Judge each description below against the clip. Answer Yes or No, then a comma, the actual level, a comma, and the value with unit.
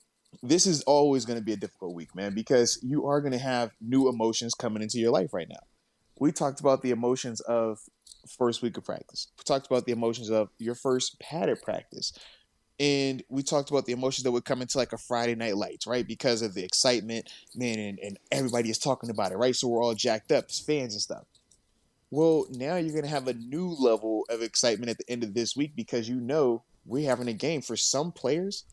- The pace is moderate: No, fast, 225 wpm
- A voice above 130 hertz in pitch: No, low, 120 Hz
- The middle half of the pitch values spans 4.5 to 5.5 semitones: No, average, 2.9 semitones